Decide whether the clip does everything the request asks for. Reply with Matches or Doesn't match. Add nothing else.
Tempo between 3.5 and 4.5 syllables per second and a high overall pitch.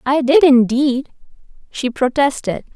Matches